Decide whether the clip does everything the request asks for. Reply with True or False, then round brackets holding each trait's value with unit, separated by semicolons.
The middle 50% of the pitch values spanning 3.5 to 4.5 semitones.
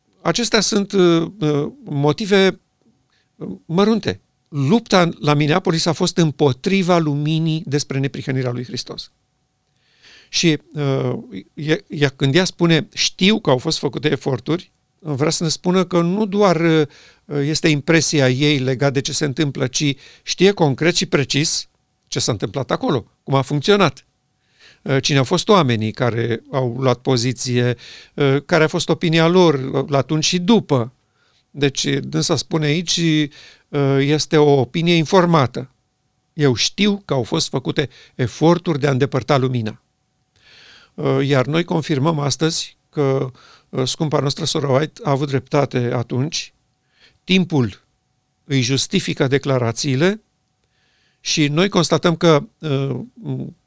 True (3.9 semitones)